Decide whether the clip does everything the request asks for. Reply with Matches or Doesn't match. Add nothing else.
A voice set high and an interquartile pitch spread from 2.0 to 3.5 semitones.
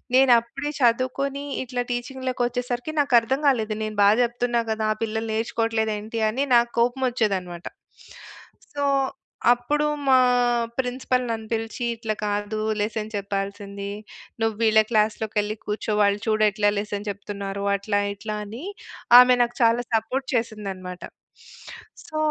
Matches